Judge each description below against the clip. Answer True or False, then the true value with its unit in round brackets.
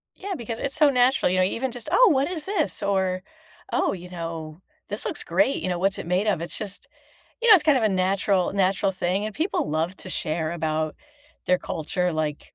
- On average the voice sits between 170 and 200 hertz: True (190 Hz)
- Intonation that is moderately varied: False (6.3 semitones)